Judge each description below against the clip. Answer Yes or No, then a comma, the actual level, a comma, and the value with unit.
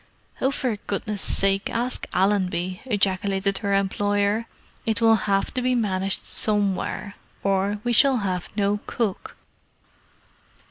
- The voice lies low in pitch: No, high, 205 Hz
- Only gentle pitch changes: Yes, narrow, 2.3 semitones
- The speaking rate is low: Yes, slow, 125 wpm